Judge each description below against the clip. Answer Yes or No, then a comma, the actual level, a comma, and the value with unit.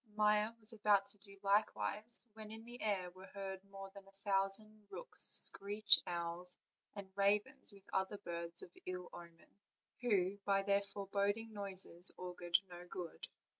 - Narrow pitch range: Yes, narrow, 2.2 semitones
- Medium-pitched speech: No, high, 200 Hz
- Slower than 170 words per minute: Yes, average, 160 wpm